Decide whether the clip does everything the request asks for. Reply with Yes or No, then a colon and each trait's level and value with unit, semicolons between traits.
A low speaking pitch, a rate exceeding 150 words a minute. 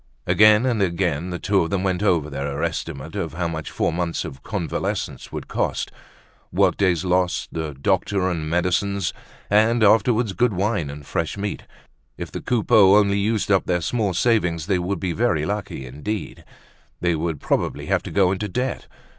Yes: very low, 95 Hz; average, 180 wpm